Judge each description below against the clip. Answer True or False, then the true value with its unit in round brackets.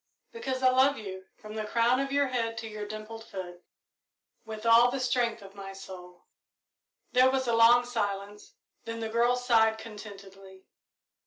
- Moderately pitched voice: False (225 Hz)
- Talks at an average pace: True (165 wpm)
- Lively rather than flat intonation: False (3.4 semitones)